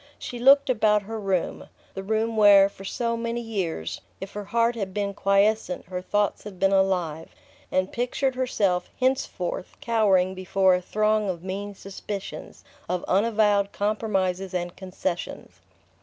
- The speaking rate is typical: Yes, average, 145 wpm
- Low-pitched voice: No, high, 200 Hz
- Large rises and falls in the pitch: No, average, 2.7 semitones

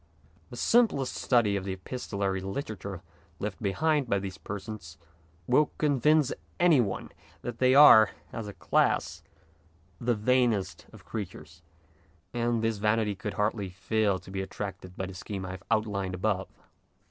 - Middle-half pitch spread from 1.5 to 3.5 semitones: No, average, 4.0 semitones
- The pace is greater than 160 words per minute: No, average, 150 wpm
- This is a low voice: Yes, low, 105 Hz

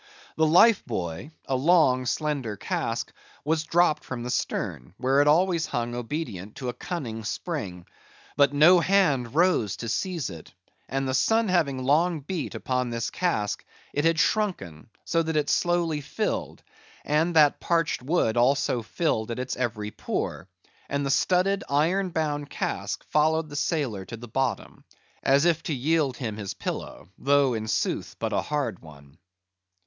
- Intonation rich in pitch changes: Yes, wide, 5.7 semitones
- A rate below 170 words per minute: Yes, average, 160 wpm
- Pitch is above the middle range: No, medium, 140 Hz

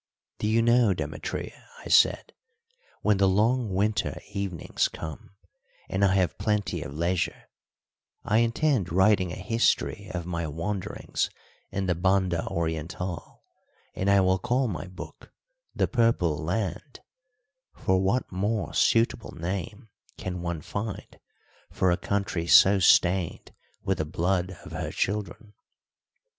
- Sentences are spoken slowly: Yes, slow, 130 wpm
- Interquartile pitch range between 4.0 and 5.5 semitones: No, average, 3.2 semitones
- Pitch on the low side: Yes, very low, 95 Hz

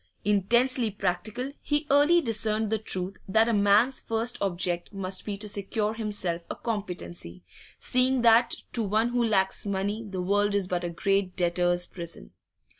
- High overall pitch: Yes, high, 205 Hz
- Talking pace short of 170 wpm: Yes, average, 160 wpm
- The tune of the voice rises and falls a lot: No, average, 3.5 semitones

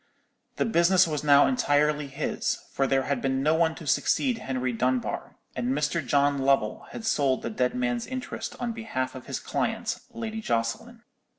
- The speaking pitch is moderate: Yes, medium, 145 Hz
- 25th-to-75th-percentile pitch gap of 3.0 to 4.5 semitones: No, average, 5.1 semitones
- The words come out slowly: No, average, 175 wpm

